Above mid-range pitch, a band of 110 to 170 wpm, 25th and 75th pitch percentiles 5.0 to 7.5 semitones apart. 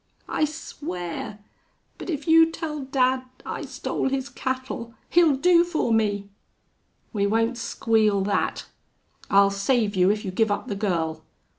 Yes: high, 230 Hz; average, 145 wpm; average, 5.3 semitones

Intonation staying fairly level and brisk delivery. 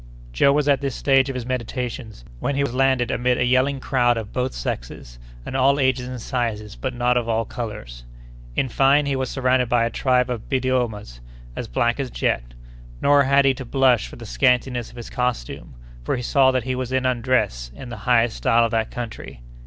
Yes: narrow, 2.3 semitones; fast, 210 wpm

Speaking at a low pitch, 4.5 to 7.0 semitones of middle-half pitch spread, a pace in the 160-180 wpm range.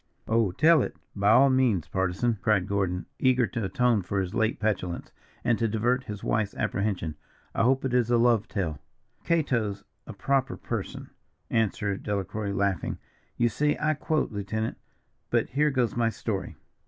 No: low, 110 Hz; average, 3.9 semitones; average, 165 wpm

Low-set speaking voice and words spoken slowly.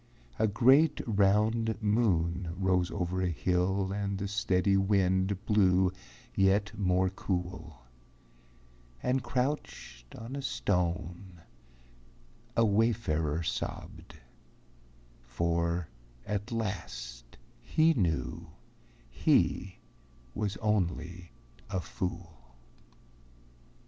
Yes: very low, 95 Hz; slow, 85 wpm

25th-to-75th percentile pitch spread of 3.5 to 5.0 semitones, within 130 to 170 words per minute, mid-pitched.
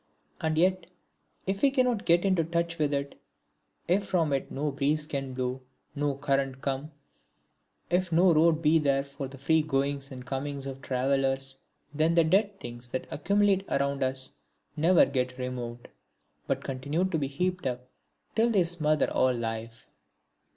Yes: average, 4.0 semitones; average, 160 wpm; medium, 145 Hz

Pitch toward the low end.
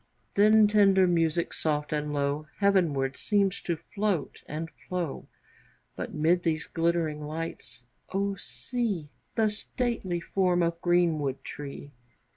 No: medium, 170 Hz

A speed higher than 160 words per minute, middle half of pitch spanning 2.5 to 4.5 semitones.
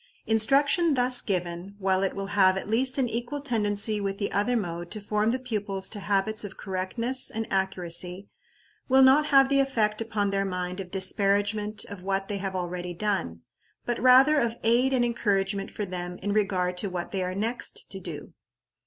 Yes: average, 190 wpm; average, 3.7 semitones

